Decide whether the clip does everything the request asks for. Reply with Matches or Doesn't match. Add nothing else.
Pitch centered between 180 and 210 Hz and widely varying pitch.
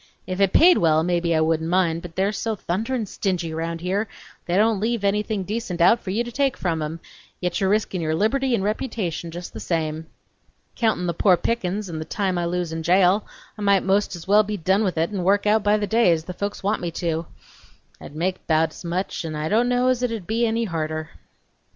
Doesn't match